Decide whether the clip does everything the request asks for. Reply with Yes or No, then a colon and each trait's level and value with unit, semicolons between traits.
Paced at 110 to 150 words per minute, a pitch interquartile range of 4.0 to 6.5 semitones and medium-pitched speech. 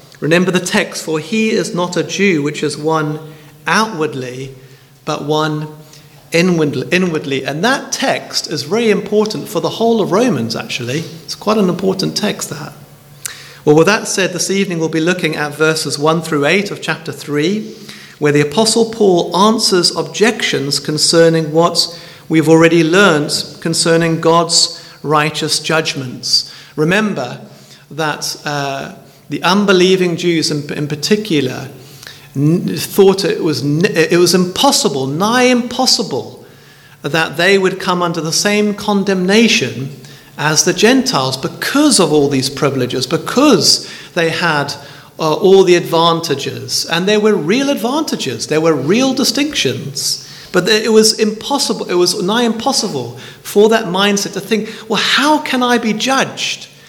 Yes: average, 140 wpm; wide, 5.5 semitones; medium, 170 Hz